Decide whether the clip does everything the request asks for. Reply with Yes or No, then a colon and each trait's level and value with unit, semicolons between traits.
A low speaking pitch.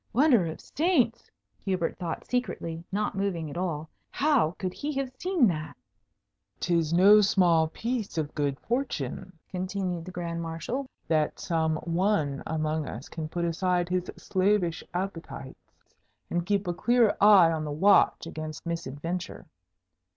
No: medium, 175 Hz